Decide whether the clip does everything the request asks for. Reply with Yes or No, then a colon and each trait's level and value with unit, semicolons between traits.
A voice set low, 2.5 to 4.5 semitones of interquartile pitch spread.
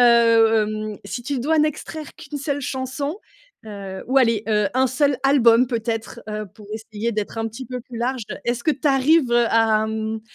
No: high, 235 Hz; average, 3.4 semitones